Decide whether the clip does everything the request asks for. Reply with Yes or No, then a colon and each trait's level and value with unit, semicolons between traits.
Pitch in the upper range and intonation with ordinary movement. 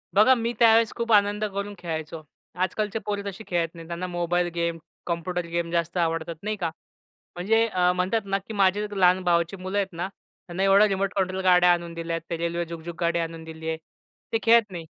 No: medium, 180 Hz; average, 3.0 semitones